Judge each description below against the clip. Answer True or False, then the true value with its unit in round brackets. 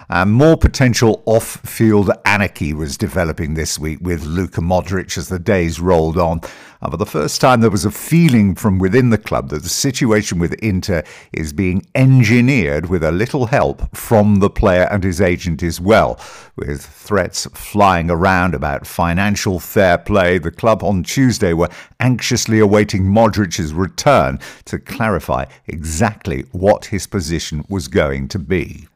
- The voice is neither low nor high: False (95 Hz)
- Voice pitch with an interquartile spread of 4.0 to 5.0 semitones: True (4.6 semitones)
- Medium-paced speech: True (160 wpm)